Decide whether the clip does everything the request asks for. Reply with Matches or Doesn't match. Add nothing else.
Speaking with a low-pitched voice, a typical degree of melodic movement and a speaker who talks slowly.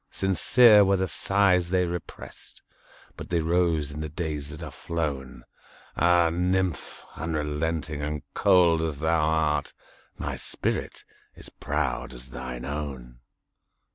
Matches